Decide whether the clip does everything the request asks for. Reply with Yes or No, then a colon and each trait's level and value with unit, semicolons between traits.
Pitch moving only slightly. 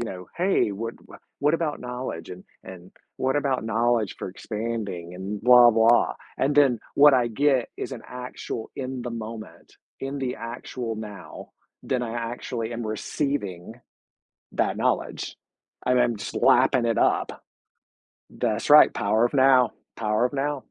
No: average, 3.1 semitones